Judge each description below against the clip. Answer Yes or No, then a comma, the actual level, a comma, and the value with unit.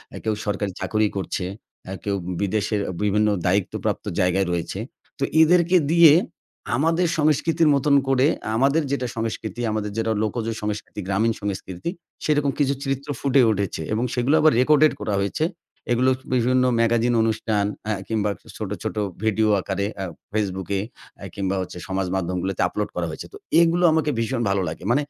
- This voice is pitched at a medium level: No, low, 110 Hz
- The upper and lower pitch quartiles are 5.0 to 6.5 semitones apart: Yes, wide, 5.6 semitones